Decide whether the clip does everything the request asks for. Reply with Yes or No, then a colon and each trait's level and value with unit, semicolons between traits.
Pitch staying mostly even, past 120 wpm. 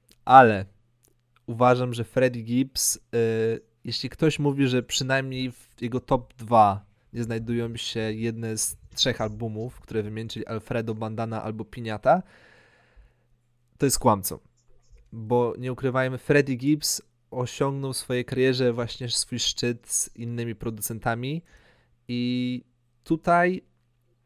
No: narrow, 2.1 semitones; average, 115 wpm